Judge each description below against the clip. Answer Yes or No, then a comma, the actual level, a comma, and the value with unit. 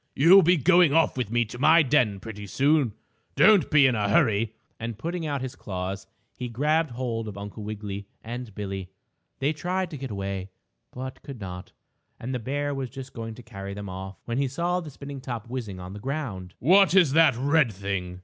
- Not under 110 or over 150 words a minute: No, average, 200 wpm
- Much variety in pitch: Yes, wide, 6.1 semitones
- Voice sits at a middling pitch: No, low, 125 Hz